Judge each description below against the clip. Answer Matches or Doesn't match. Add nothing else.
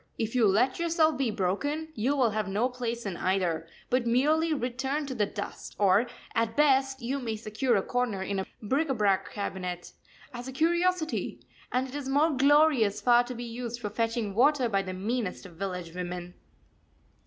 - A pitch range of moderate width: Matches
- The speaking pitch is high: Matches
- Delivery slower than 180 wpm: Doesn't match